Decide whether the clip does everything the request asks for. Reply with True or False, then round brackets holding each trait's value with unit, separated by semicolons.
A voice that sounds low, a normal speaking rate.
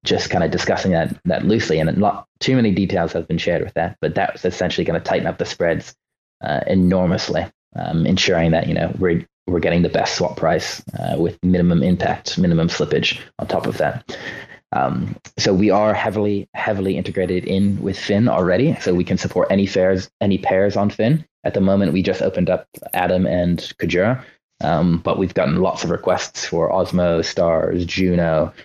True (95 Hz; 195 wpm)